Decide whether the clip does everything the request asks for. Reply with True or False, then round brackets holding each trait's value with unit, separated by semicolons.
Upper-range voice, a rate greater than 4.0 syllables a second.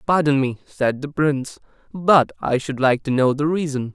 False (145 Hz; 4.8 syllables/s)